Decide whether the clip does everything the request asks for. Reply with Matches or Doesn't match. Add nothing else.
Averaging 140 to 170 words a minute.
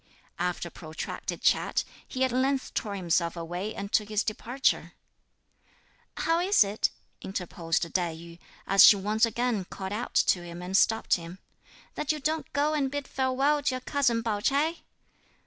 Matches